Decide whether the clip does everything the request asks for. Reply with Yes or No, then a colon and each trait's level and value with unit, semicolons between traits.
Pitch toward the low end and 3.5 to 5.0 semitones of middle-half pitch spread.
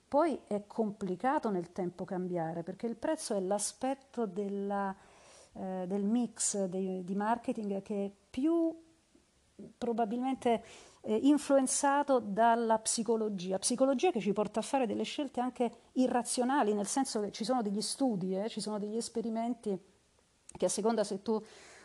No: high, 225 Hz; average, 4.1 semitones